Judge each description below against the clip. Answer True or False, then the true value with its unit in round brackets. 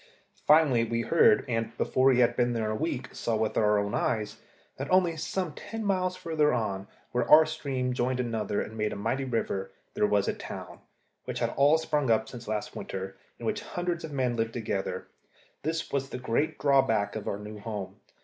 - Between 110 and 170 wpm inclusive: False (200 wpm)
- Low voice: True (125 Hz)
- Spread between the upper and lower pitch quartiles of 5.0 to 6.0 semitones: True (5.6 semitones)